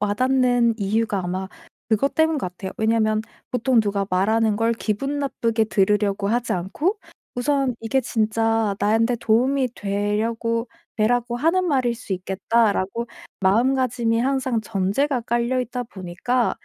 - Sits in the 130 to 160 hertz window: No, high, 230 Hz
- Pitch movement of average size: Yes, average, 3.3 semitones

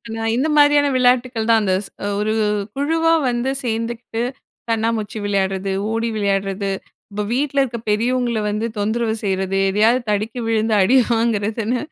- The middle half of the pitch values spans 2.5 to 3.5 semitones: Yes, average, 2.9 semitones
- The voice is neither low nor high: No, high, 225 Hz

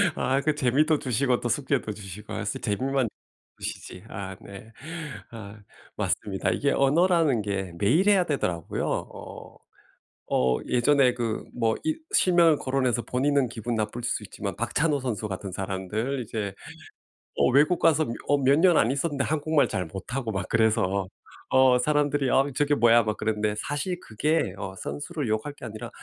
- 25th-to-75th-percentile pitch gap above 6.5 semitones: No, wide, 5.5 semitones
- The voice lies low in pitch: Yes, low, 125 Hz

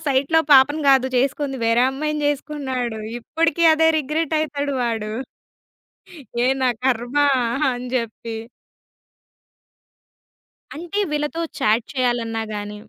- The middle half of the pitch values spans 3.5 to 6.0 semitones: Yes, average, 3.8 semitones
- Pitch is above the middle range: Yes, very high, 270 Hz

